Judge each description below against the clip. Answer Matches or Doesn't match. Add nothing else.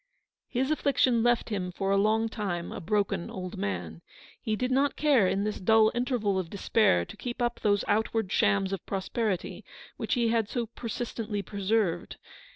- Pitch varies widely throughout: Doesn't match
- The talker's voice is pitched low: Doesn't match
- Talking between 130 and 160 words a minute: Doesn't match